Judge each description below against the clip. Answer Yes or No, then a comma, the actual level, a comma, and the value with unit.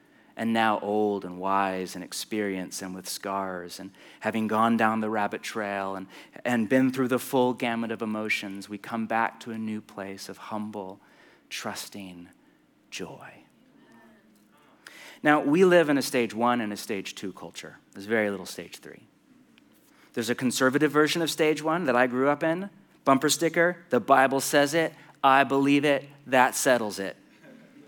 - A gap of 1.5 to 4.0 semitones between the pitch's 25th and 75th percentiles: No, average, 5.3 semitones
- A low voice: Yes, low, 115 Hz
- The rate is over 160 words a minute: Yes, average, 170 wpm